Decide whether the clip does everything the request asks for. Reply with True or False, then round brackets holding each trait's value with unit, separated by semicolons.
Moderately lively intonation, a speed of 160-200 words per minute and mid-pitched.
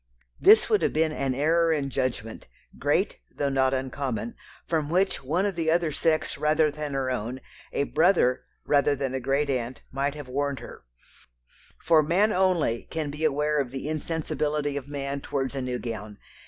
True (3.1 semitones; 180 wpm; 145 Hz)